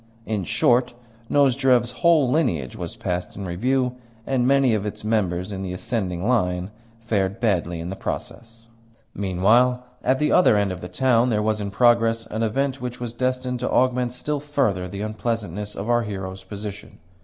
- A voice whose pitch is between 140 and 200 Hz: No, low, 115 Hz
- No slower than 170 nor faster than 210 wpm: Yes, average, 175 wpm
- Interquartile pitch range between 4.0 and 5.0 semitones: Yes, average, 4.4 semitones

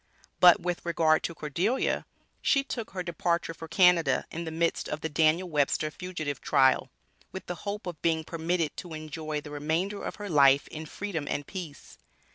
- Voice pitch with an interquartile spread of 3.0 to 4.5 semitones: No, narrow, 2.6 semitones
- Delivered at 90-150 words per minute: No, average, 180 wpm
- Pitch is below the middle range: No, medium, 165 Hz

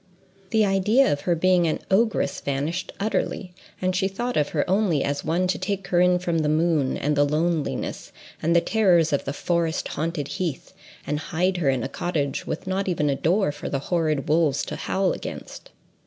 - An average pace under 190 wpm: No, average, 200 wpm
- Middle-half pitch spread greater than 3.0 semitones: Yes, average, 3.9 semitones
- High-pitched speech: No, medium, 170 Hz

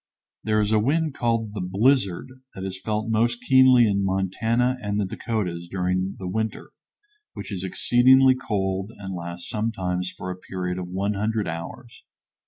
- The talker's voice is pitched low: Yes, low, 105 Hz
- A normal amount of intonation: Yes, average, 3.9 semitones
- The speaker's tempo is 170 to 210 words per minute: No, average, 160 wpm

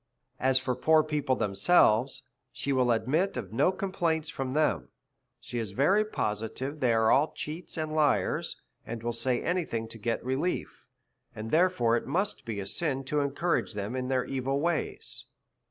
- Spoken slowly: No, average, 170 wpm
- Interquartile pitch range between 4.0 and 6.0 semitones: Yes, average, 5.0 semitones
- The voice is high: No, low, 130 Hz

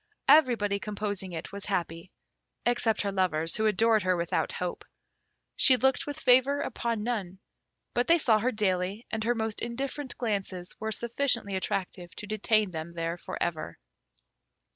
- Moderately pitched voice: No, high, 210 Hz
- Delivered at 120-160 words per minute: Yes, average, 155 wpm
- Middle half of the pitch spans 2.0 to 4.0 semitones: No, average, 4.5 semitones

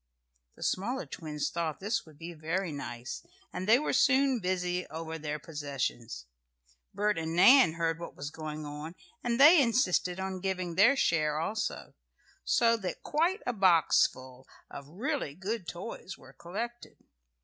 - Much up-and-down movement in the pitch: Yes, wide, 6.4 semitones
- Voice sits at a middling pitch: Yes, medium, 175 Hz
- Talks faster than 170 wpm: No, average, 155 wpm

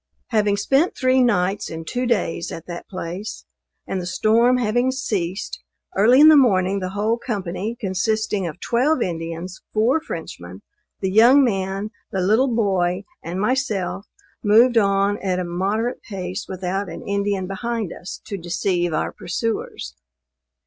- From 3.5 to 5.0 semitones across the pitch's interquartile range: Yes, average, 4.2 semitones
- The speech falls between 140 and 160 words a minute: Yes, average, 150 wpm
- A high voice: Yes, high, 200 Hz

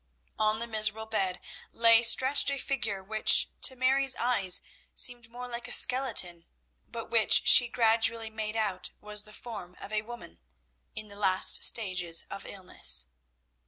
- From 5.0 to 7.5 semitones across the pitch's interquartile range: No, average, 3.3 semitones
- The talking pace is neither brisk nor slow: Yes, average, 155 wpm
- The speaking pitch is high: Yes, high, 220 Hz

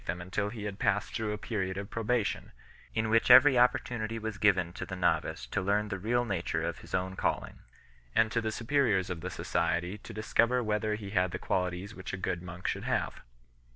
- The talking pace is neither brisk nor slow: No, fast, 210 wpm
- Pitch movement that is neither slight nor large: Yes, average, 3.2 semitones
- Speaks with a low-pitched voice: Yes, low, 105 Hz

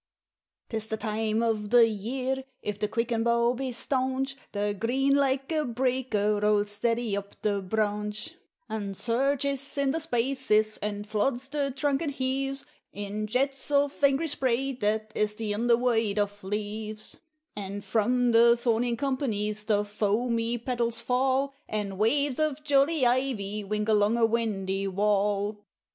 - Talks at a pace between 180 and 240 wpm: No, average, 150 wpm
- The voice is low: No, high, 230 Hz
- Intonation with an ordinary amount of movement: Yes, average, 4.1 semitones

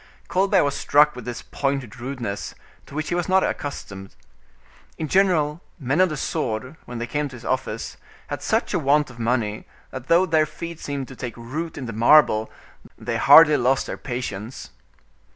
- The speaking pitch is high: No, low, 135 Hz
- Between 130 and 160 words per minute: No, average, 185 wpm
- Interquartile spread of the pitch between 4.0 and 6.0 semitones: Yes, average, 4.3 semitones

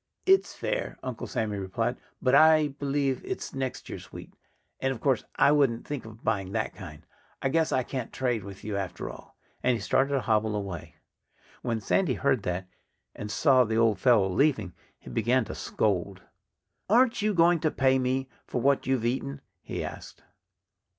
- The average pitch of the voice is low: Yes, low, 125 Hz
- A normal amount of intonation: Yes, average, 4.5 semitones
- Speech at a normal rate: Yes, average, 180 wpm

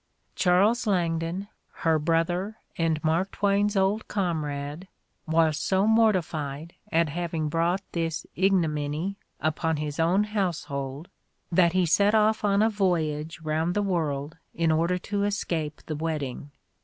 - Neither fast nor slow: No, slow, 130 wpm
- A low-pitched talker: No, medium, 170 Hz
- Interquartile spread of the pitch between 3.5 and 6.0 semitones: Yes, average, 3.9 semitones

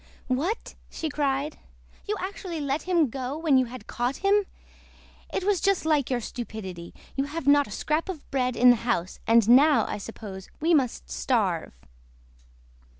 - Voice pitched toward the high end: Yes, very high, 275 Hz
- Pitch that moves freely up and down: No, average, 5.0 semitones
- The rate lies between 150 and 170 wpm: Yes, average, 165 wpm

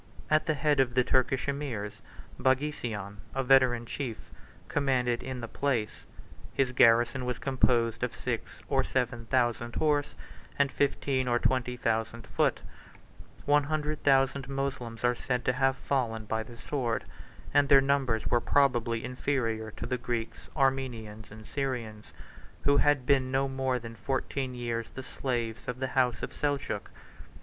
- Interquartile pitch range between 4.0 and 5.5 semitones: No, average, 2.8 semitones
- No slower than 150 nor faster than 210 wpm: Yes, average, 155 wpm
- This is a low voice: Yes, low, 125 Hz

